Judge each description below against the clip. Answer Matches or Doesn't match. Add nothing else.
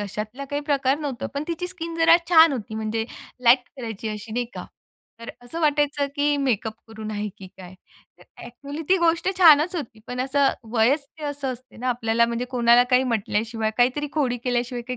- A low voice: Doesn't match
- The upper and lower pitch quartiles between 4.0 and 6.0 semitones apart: Matches